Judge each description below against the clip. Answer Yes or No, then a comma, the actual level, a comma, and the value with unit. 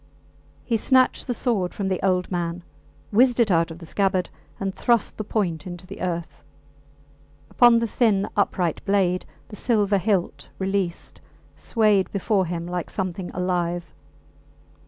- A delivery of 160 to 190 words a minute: No, average, 145 wpm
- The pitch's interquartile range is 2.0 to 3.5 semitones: Yes, average, 3.2 semitones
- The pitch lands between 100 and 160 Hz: No, high, 190 Hz